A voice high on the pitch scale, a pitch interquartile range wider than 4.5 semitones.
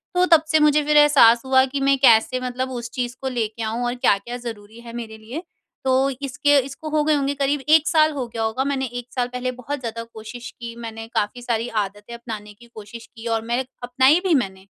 No: high, 245 Hz; average, 3.5 semitones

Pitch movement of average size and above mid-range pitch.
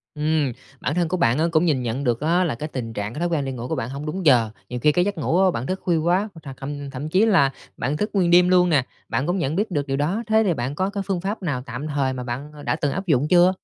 No: average, 4.9 semitones; medium, 155 Hz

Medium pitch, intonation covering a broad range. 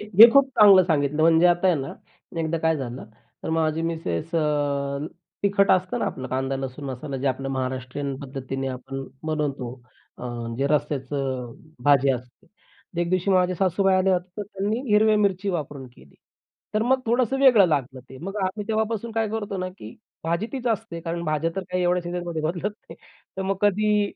Yes: medium, 165 Hz; wide, 6.4 semitones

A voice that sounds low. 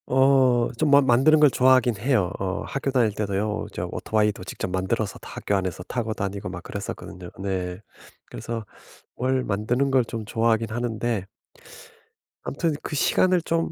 Yes: low, 115 Hz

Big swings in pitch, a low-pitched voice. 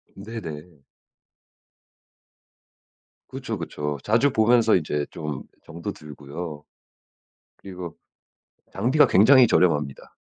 Yes: wide, 6.8 semitones; very low, 90 Hz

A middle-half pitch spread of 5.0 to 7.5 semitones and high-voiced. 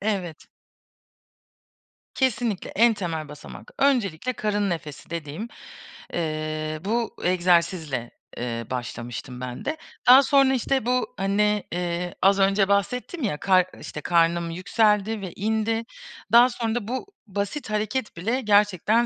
Yes: average, 5.3 semitones; high, 200 Hz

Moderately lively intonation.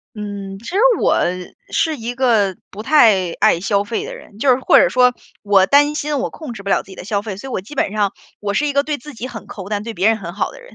Yes: average, 4.7 semitones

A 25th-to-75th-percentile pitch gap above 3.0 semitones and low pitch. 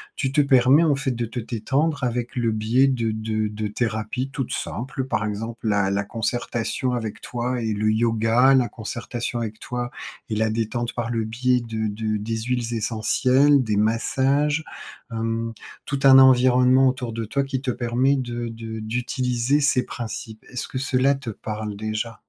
No: average, 2.7 semitones; low, 120 Hz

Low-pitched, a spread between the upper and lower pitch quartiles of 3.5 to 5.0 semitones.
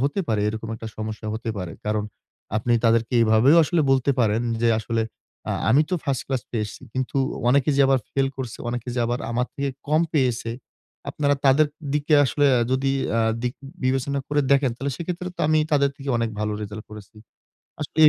Yes: low, 130 Hz; average, 3.9 semitones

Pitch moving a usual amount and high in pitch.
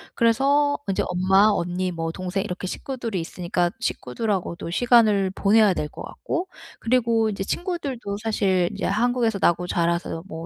Yes: average, 4.6 semitones; high, 200 Hz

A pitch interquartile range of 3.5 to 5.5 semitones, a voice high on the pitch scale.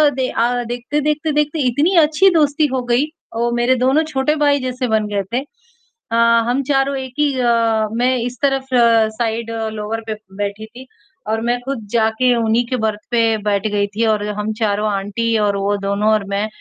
Yes: average, 4.1 semitones; high, 235 Hz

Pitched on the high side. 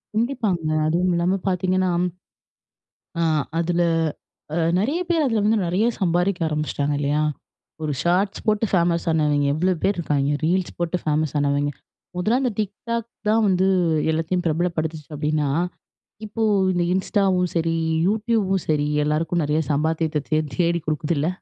No: medium, 175 Hz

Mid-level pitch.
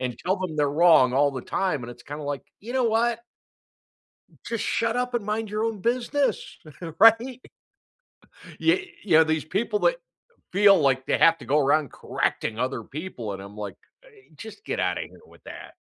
Yes: medium, 180 Hz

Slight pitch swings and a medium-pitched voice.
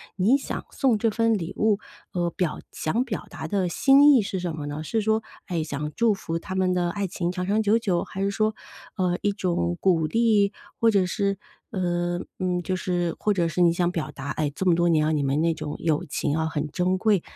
No: average, 3.7 semitones; medium, 180 Hz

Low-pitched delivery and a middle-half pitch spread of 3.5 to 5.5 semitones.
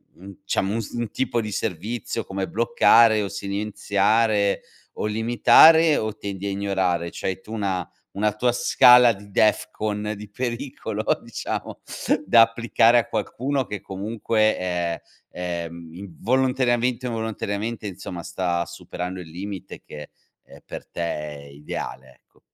Yes: low, 105 Hz; average, 3.8 semitones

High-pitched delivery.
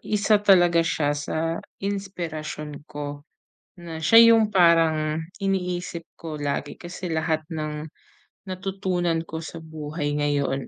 No: medium, 165 Hz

